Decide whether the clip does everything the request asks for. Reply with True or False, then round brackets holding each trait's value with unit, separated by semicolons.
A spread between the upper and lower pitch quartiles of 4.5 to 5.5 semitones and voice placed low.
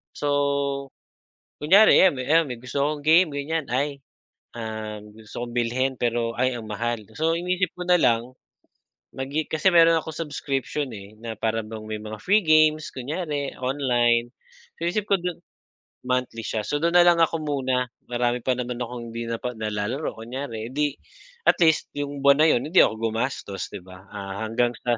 True (4.8 semitones; 130 Hz)